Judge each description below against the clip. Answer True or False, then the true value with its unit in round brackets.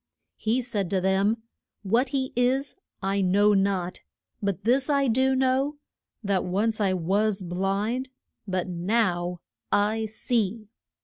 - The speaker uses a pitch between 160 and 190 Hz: False (210 Hz)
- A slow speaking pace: True (130 wpm)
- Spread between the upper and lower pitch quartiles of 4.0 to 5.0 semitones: True (4.3 semitones)